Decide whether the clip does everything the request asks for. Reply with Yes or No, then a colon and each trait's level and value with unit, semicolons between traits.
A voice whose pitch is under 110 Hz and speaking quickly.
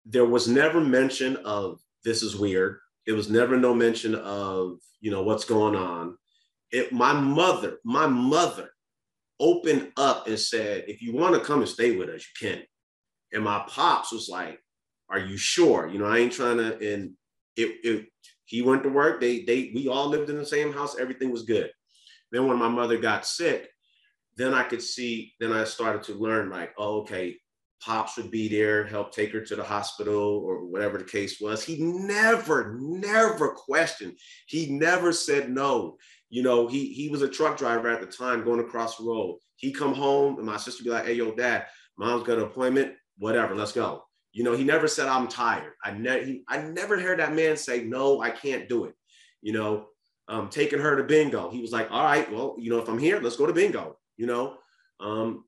No: low, 120 Hz; fast, 210 wpm